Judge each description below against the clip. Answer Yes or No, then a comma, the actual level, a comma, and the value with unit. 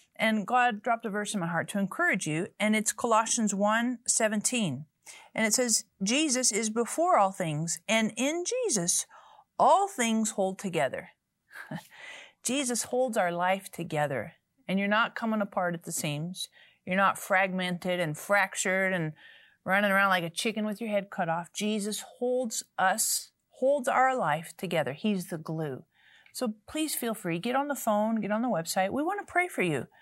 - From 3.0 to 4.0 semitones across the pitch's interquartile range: No, average, 4.9 semitones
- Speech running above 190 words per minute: No, average, 175 wpm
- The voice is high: Yes, high, 210 Hz